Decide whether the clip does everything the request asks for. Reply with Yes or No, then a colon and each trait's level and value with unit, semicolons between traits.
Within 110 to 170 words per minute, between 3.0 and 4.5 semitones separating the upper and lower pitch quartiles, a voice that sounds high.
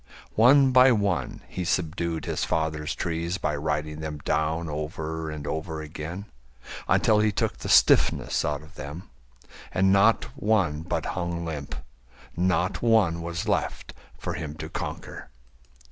No: average, 145 wpm; average, 3.8 semitones; very low, 85 Hz